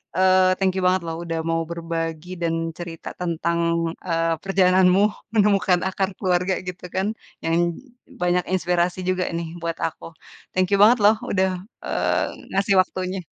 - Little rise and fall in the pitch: Yes, narrow, 1.9 semitones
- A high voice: No, medium, 180 Hz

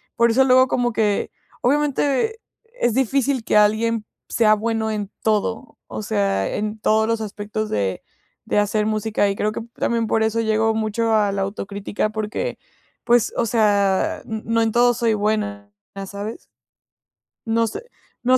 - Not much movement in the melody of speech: Yes, narrow, 1.9 semitones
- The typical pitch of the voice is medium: No, high, 220 Hz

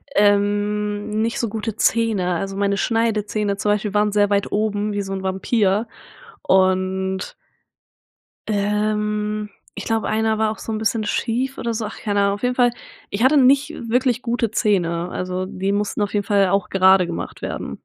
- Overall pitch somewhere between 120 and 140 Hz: No, high, 210 Hz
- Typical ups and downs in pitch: No, narrow, 2.0 semitones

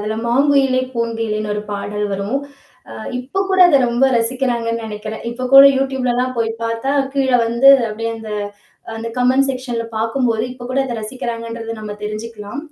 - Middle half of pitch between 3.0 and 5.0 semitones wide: No, narrow, 2.5 semitones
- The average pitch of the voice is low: No, high, 230 Hz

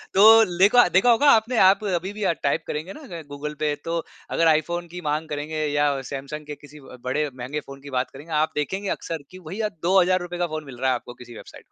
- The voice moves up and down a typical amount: Yes, average, 4.2 semitones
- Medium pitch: Yes, medium, 155 Hz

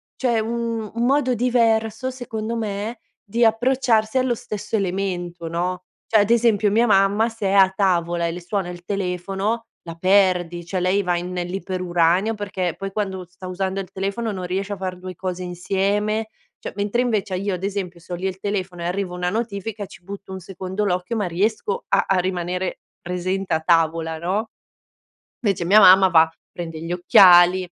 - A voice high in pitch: Yes, high, 195 Hz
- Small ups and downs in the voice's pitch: No, average, 3.2 semitones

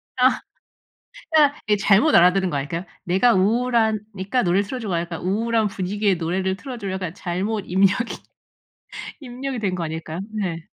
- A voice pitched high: Yes, high, 195 Hz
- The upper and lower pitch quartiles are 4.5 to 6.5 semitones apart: No, average, 4.1 semitones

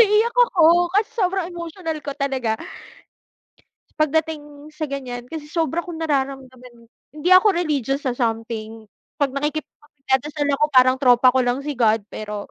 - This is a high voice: Yes, very high, 285 Hz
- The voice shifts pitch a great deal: No, average, 4.3 semitones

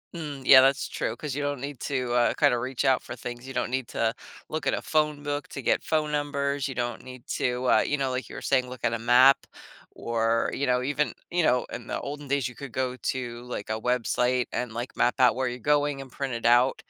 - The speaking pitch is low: Yes, low, 130 Hz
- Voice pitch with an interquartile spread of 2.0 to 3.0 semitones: Yes, narrow, 2.5 semitones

